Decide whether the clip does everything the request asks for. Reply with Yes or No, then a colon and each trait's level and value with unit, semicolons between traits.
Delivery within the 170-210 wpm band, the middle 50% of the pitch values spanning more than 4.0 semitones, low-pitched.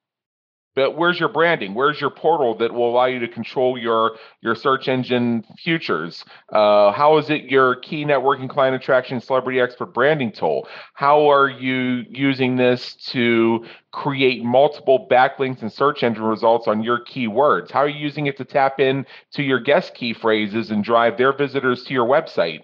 No: average, 180 wpm; average, 3.0 semitones; low, 130 Hz